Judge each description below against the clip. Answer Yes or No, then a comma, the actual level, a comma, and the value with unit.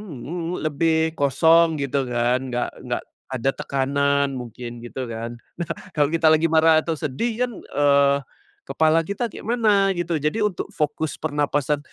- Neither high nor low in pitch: Yes, medium, 150 Hz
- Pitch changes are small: No, average, 3.6 semitones